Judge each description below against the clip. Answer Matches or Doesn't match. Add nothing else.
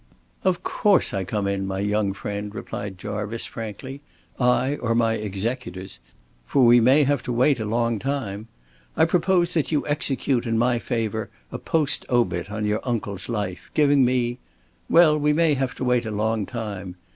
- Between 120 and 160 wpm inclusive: Doesn't match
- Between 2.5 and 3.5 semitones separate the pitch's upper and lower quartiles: Doesn't match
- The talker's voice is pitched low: Matches